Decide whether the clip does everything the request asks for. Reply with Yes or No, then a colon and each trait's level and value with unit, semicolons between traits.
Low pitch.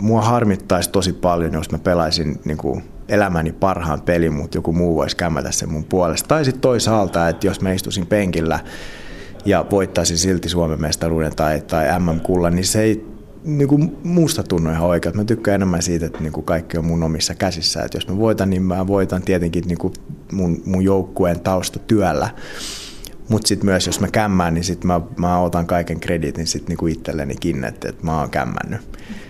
Yes: very low, 90 Hz